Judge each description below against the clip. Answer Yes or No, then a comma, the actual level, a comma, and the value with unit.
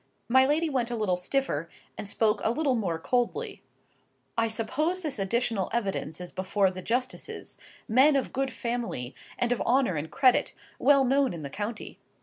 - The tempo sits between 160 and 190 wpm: Yes, average, 170 wpm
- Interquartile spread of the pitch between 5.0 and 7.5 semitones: Yes, wide, 5.4 semitones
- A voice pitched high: Yes, high, 235 Hz